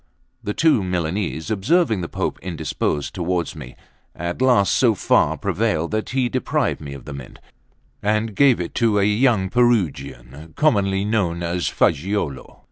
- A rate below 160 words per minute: Yes, average, 150 wpm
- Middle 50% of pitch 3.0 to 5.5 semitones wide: Yes, average, 5.1 semitones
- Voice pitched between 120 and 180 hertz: No, very low, 95 Hz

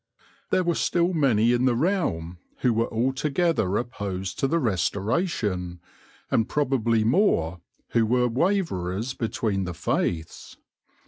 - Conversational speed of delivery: No, slow, 125 wpm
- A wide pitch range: Yes, wide, 6.8 semitones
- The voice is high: No, low, 115 Hz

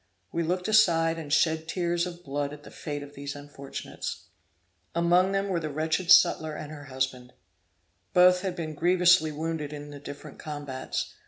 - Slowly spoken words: No, average, 170 wpm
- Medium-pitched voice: Yes, medium, 160 Hz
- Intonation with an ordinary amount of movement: Yes, average, 3.2 semitones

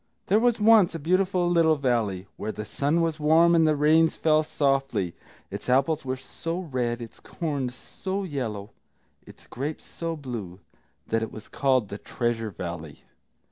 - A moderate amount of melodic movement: No, wide, 5.9 semitones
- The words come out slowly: No, average, 170 wpm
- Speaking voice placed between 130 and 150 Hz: Yes, medium, 140 Hz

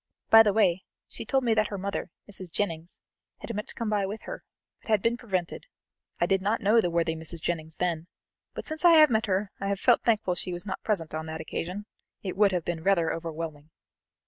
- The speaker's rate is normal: No, fast, 225 wpm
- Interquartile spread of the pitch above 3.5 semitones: Yes, average, 4.2 semitones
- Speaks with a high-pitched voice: Yes, high, 195 Hz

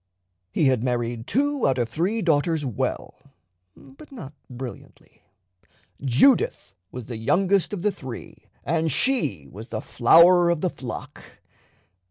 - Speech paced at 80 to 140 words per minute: Yes, slow, 135 wpm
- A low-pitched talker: No, medium, 145 Hz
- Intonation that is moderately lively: No, wide, 7.1 semitones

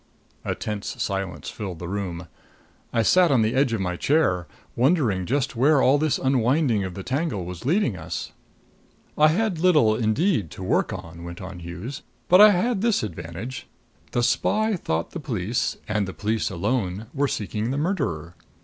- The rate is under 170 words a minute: No, average, 175 wpm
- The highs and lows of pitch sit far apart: Yes, wide, 8.0 semitones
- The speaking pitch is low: Yes, low, 115 Hz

